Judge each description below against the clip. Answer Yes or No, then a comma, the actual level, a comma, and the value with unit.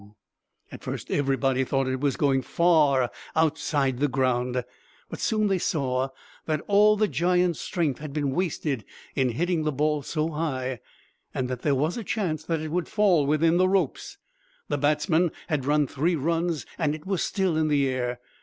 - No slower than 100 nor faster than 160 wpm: No, average, 180 wpm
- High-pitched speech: No, medium, 150 Hz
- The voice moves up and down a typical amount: Yes, average, 4.1 semitones